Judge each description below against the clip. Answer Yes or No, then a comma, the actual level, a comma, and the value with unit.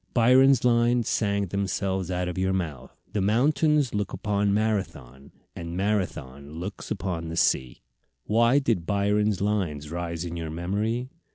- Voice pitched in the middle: No, low, 100 Hz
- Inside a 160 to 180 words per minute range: No, average, 145 wpm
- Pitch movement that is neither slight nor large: Yes, average, 4.4 semitones